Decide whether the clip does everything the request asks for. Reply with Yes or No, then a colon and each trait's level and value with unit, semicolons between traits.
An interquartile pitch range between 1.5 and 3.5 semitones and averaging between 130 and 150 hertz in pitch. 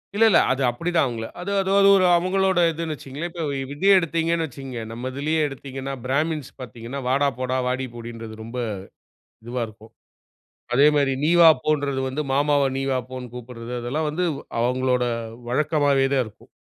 No: average, 4.0 semitones; low, 135 Hz